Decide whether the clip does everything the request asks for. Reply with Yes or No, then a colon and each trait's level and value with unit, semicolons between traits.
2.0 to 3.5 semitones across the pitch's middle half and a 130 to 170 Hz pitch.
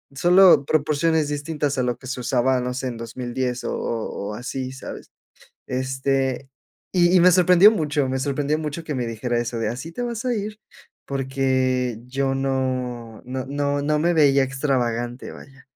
Yes: average, 3.1 semitones; low, 135 Hz